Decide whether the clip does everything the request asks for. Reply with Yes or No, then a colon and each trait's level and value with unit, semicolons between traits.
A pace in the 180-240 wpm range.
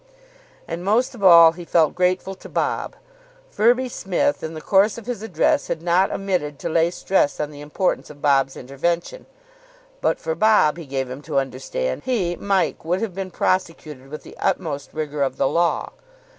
Yes: average, 185 wpm